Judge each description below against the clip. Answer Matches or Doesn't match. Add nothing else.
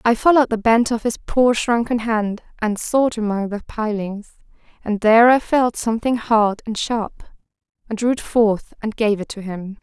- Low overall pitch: Doesn't match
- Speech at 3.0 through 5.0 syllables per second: Matches